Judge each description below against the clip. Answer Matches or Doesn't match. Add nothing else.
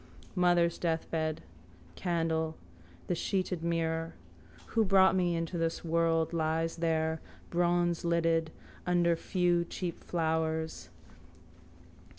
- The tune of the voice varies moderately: Doesn't match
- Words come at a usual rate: Doesn't match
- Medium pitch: Matches